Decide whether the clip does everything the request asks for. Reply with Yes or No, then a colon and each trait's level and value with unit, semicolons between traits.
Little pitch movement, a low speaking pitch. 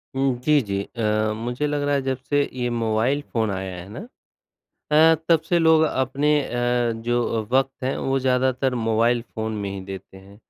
No: average, 3.6 semitones; low, 120 Hz